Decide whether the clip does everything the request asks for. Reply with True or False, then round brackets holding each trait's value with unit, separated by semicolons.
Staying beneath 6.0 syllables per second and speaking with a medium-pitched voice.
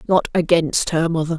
True (5.0 syllables/s; 165 Hz)